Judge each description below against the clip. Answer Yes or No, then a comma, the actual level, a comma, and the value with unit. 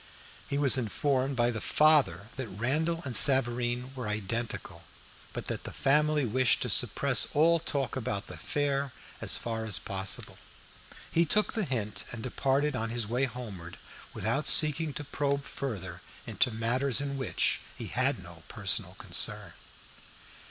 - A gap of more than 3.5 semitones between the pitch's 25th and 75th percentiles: Yes, average, 3.9 semitones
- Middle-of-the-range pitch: No, low, 130 Hz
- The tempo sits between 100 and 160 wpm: Yes, average, 150 wpm